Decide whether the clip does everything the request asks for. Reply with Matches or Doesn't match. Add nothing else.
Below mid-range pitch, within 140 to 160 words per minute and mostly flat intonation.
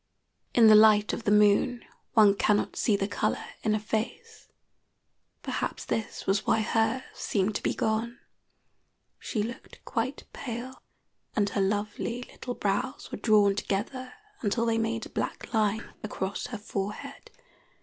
Doesn't match